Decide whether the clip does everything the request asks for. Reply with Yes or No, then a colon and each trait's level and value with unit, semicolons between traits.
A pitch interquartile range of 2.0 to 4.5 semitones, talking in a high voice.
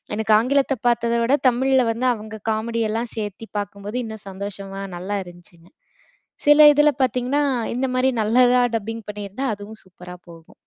Yes: average, 3.7 semitones; high, 220 Hz